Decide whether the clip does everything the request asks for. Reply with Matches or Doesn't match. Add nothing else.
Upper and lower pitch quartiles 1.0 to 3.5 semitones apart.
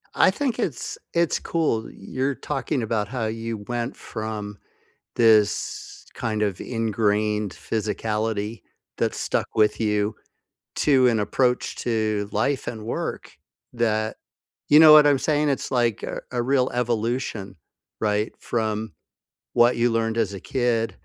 Matches